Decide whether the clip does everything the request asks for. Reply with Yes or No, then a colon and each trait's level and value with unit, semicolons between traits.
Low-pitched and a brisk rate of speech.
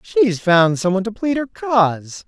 No: high, 190 Hz; fast, 210 wpm